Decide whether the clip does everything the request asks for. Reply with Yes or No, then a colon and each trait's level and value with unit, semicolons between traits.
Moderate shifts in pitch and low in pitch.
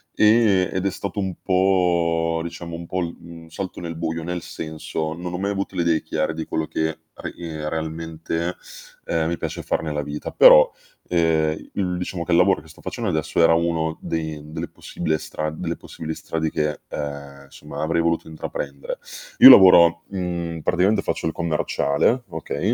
No: narrow, 2.1 semitones; very low, 85 Hz